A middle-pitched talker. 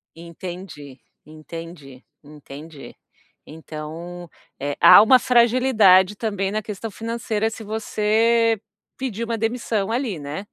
No: high, 200 Hz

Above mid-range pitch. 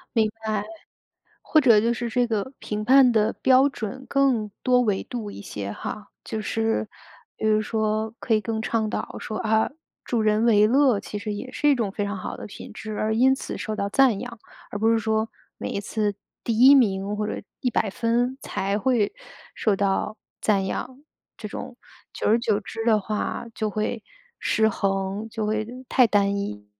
Yes: high, 220 Hz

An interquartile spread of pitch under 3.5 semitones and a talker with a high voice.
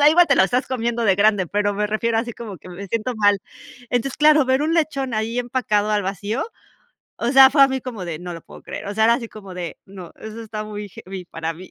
No: average, 4.3 semitones; high, 215 Hz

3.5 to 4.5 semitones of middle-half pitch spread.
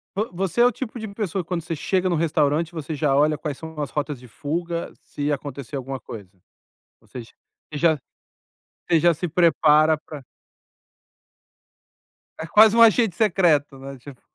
Yes: average, 3.8 semitones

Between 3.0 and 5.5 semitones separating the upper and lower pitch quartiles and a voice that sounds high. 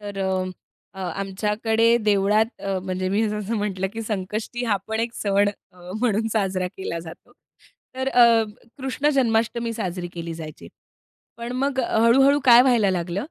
Yes: average, 3.6 semitones; high, 210 Hz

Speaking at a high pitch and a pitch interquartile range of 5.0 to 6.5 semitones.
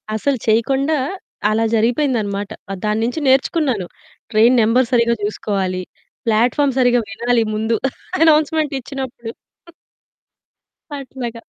No: high, 235 Hz; average, 3.5 semitones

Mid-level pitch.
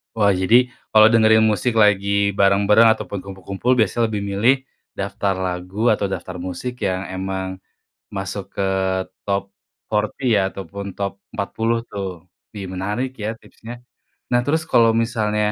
No: low, 100 Hz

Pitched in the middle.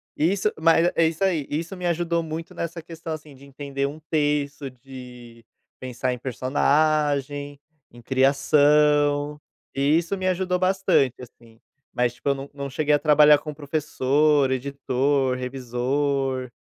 Yes: medium, 145 Hz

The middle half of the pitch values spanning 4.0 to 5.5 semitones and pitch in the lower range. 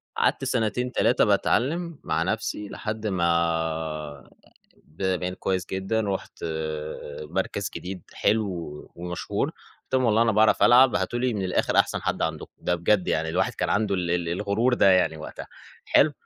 Yes: average, 4.6 semitones; very low, 95 Hz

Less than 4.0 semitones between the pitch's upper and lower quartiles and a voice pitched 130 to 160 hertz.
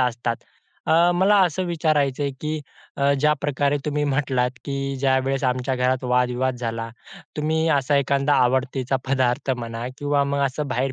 Yes: narrow, 2.6 semitones; low, 135 Hz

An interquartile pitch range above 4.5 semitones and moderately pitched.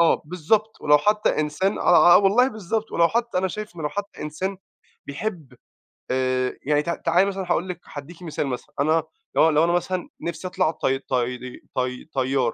Yes: average, 5.2 semitones; medium, 170 Hz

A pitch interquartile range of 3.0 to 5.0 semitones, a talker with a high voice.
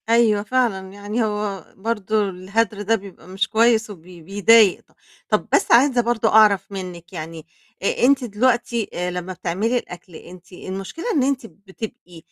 Yes: average, 3.7 semitones; high, 205 Hz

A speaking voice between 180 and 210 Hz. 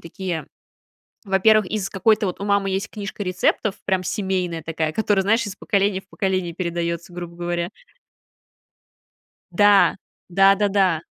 Yes: high, 190 Hz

